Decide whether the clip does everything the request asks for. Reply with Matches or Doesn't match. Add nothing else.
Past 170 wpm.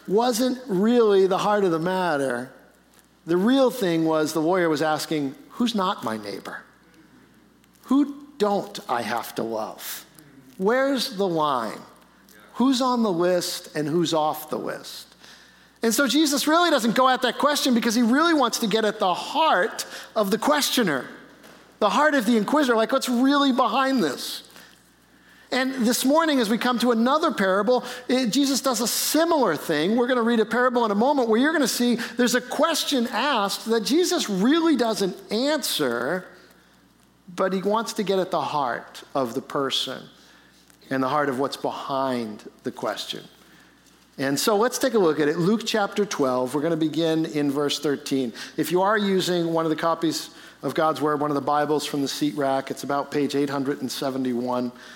Matches